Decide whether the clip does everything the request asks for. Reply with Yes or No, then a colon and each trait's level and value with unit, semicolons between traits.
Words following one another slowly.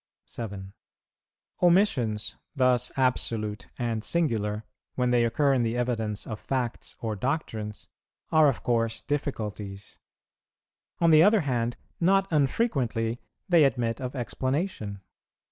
Yes: slow, 115 wpm